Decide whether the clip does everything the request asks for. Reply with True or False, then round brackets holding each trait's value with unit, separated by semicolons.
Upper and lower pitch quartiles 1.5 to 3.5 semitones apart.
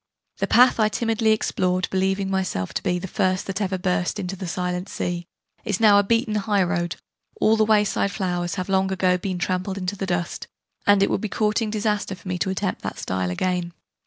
True (2.4 semitones)